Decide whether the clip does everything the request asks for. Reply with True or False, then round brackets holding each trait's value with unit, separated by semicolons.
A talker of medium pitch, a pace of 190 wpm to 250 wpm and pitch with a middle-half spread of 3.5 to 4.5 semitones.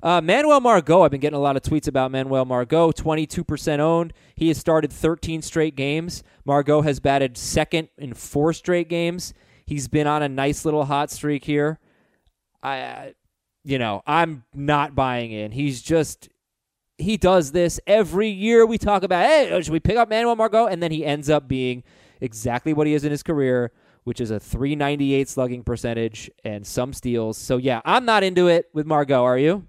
True (150 Hz; 195 wpm; 4.2 semitones)